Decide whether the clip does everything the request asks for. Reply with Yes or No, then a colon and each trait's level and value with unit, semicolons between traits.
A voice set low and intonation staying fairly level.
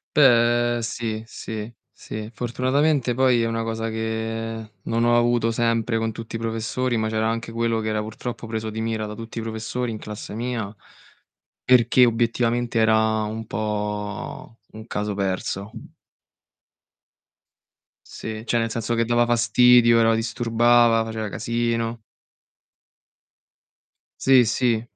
Yes: low, 115 Hz; narrow, 1.2 semitones